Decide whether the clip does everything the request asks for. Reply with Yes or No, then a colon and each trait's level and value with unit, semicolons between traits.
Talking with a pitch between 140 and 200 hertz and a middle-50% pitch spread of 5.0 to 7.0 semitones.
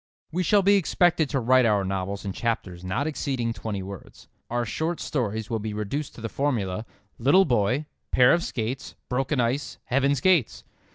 No: low, 125 Hz; average, 5.3 semitones